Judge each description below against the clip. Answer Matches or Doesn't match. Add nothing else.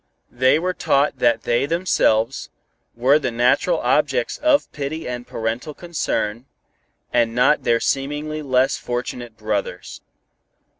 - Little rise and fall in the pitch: Doesn't match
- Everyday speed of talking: Doesn't match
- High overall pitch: Doesn't match